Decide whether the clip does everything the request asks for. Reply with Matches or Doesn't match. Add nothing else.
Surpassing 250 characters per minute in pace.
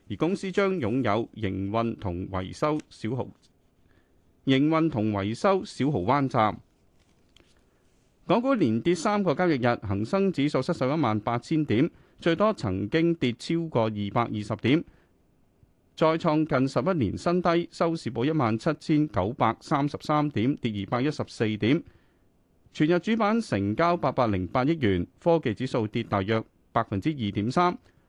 Doesn't match